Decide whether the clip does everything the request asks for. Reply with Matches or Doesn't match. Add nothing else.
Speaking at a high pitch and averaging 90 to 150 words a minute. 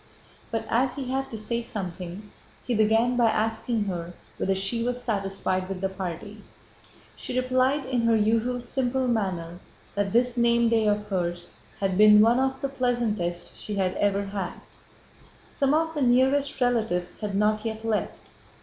Doesn't match